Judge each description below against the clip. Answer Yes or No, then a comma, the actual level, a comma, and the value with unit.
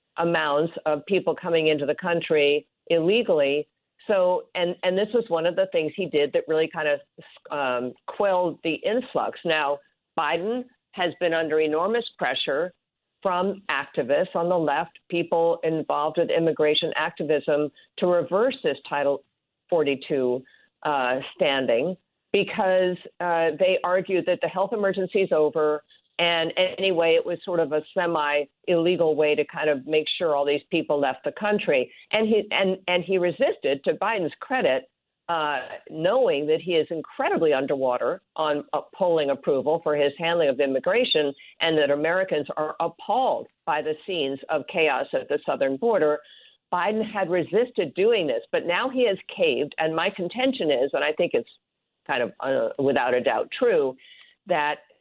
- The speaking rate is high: No, average, 160 wpm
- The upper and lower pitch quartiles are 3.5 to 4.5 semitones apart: Yes, average, 4.2 semitones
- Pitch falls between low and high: Yes, medium, 170 Hz